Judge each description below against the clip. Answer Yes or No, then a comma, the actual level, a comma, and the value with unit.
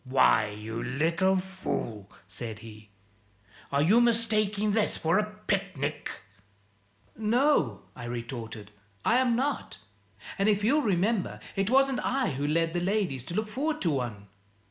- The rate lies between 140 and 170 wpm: Yes, average, 145 wpm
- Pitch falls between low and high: Yes, medium, 180 Hz